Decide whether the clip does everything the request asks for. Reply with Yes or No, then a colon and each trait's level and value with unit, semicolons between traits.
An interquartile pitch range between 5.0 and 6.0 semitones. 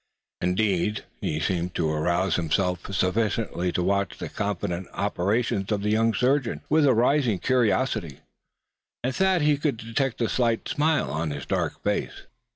Yes: wide, 5.6 semitones